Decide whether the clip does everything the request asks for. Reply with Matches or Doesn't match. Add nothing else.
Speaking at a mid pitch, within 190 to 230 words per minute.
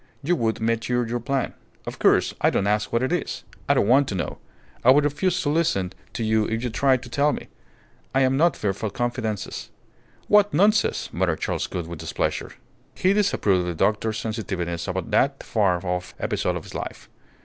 Doesn't match